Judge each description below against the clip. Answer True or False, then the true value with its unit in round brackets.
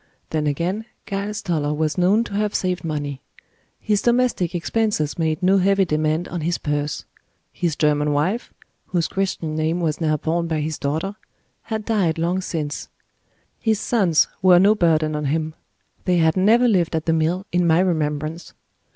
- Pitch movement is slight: False (3.9 semitones)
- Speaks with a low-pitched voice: False (170 Hz)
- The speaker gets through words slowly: False (170 wpm)